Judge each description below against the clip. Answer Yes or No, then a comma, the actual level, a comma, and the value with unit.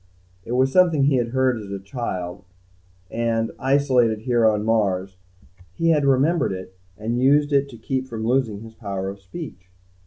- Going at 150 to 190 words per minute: Yes, average, 175 wpm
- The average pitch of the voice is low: Yes, low, 115 Hz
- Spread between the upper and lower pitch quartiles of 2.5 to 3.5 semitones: No, average, 4.7 semitones